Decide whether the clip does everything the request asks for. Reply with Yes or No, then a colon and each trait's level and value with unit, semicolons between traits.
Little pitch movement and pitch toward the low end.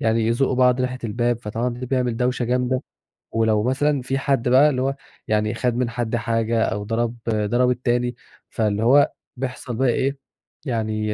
Yes: narrow, 2.1 semitones; low, 120 Hz